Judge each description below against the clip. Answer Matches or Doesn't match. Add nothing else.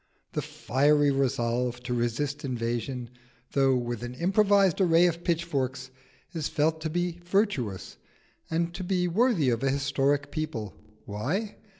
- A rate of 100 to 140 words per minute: Matches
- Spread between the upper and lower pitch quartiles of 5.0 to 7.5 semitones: Matches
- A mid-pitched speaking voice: Matches